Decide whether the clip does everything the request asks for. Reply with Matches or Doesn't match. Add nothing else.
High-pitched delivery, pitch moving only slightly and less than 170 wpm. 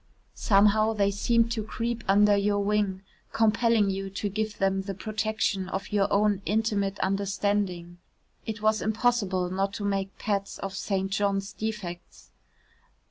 Matches